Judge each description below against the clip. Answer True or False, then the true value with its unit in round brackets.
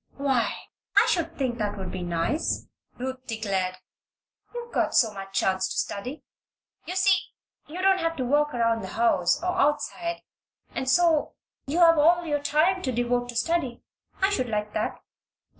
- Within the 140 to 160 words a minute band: False (170 wpm)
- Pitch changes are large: True (7.0 semitones)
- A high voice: True (265 Hz)